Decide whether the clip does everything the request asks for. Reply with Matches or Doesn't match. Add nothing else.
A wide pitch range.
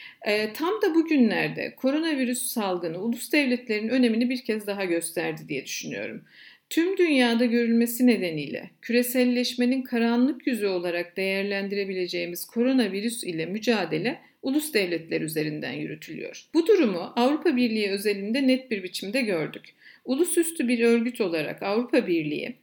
Doesn't match